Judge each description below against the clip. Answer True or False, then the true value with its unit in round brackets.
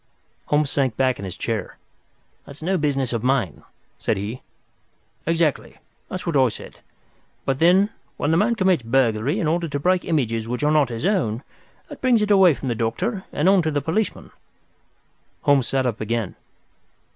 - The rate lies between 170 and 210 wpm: True (180 wpm)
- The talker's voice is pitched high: False (145 Hz)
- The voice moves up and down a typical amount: False (6.6 semitones)